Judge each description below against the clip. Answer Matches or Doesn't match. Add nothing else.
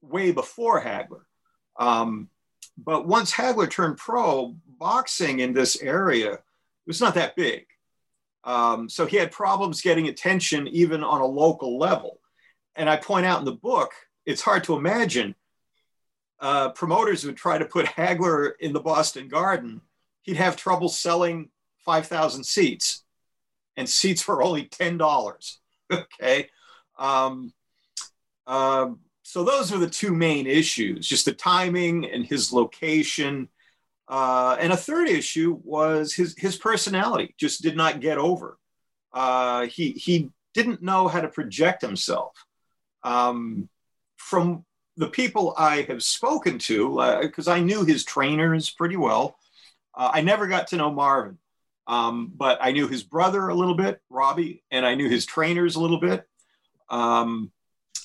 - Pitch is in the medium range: Matches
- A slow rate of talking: Doesn't match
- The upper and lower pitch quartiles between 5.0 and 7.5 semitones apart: Matches